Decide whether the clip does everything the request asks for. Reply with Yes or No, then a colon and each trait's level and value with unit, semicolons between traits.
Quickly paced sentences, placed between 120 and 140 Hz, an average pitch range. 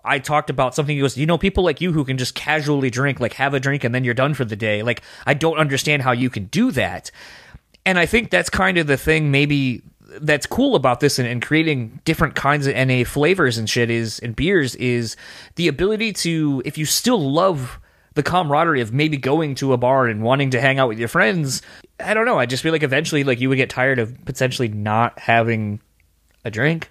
Yes: fast, 235 wpm; low, 135 Hz; average, 4.0 semitones